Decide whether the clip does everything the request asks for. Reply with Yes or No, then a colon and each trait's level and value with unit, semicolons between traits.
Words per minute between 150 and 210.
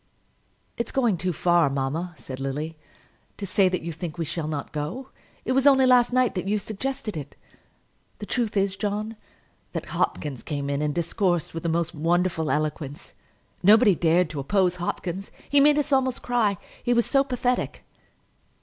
Yes: average, 175 wpm